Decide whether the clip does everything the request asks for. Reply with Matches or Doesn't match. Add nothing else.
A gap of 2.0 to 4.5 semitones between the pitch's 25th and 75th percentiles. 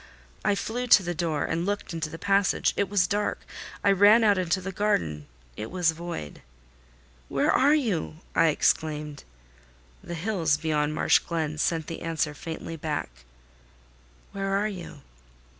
Doesn't match